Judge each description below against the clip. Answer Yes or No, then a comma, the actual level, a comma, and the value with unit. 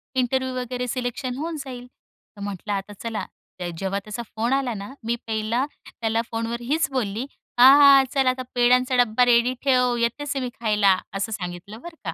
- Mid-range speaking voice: No, high, 240 Hz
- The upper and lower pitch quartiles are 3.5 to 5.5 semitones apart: No, average, 3.0 semitones